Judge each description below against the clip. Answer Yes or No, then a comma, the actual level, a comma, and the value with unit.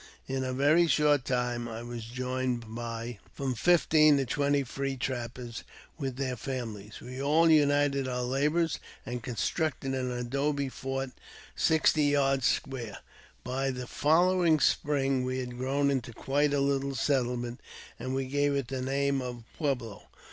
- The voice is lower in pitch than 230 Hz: Yes, low, 135 Hz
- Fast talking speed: No, average, 155 wpm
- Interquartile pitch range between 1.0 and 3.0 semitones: Yes, narrow, 2.5 semitones